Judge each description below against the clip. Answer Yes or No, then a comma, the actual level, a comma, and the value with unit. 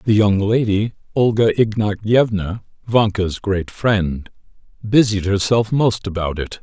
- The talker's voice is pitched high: No, low, 105 Hz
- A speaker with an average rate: No, slow, 120 wpm